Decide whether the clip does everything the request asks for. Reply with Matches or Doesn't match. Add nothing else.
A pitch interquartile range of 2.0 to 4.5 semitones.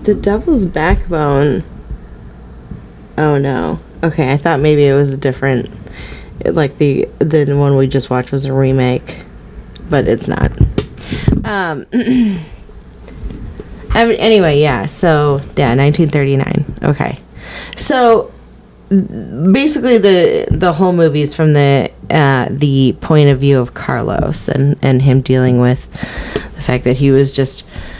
Matches